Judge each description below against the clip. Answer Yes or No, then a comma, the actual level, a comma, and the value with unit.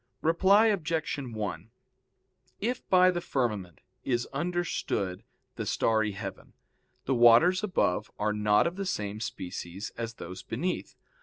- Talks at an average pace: No, slow, 130 wpm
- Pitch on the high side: No, low, 120 Hz